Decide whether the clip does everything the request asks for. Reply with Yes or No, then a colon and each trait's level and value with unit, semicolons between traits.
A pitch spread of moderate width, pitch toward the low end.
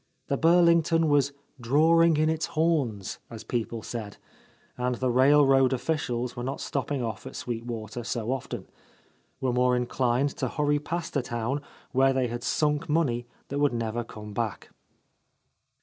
Yes: average, 3.7 semitones; low, 130 Hz